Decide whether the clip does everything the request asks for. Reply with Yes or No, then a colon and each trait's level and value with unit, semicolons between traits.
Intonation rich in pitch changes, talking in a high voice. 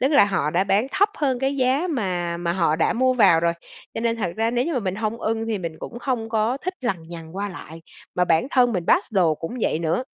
Yes: wide, 6.5 semitones; high, 215 Hz